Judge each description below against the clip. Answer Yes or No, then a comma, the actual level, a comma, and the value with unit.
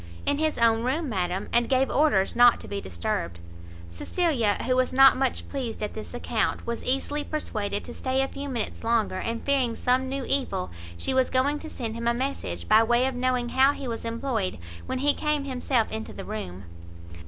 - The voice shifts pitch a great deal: No, average, 3.4 semitones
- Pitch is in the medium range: No, high, 245 Hz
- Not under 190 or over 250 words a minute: Yes, average, 200 wpm